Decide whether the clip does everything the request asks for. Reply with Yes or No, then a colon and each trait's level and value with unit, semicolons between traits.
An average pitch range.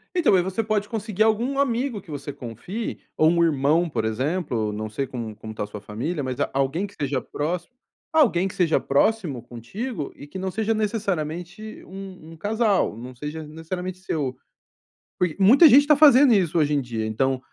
No: wide, 7.9 semitones